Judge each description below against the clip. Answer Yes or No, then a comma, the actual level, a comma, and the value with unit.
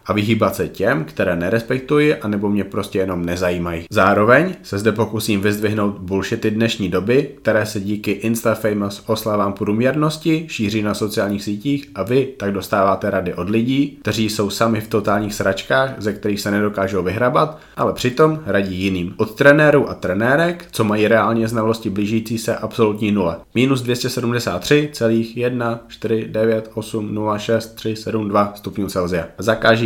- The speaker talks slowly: No, average, 135 wpm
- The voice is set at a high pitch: No, low, 110 Hz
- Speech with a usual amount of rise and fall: No, narrow, 2.2 semitones